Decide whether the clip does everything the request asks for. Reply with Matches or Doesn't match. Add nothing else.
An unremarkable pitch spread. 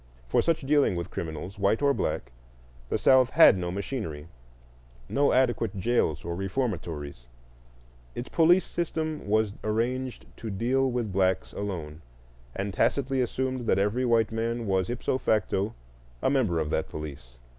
Doesn't match